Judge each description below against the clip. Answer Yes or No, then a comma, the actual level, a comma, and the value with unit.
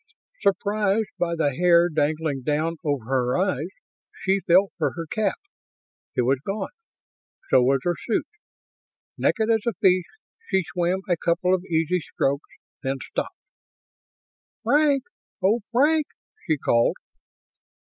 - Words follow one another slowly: Yes, slow, 130 wpm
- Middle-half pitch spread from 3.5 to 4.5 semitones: No, average, 5.1 semitones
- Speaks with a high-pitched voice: No, medium, 175 Hz